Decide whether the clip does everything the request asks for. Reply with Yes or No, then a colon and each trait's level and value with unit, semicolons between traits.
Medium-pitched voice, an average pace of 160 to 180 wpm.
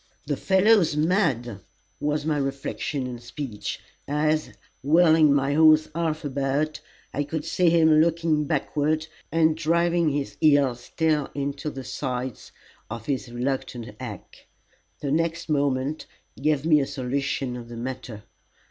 No: medium, 145 Hz; slow, 135 wpm